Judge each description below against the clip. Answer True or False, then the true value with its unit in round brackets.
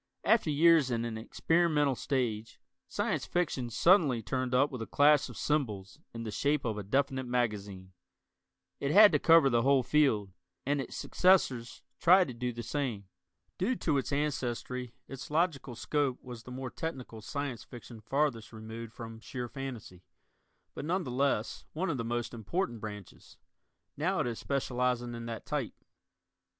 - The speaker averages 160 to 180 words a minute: True (165 wpm)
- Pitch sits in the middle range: False (125 Hz)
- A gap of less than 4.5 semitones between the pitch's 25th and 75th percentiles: True (4.0 semitones)